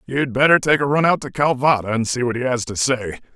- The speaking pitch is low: Yes, low, 130 Hz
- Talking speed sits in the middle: No, fast, 270 wpm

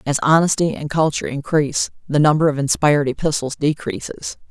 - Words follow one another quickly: No, average, 145 wpm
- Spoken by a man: No, female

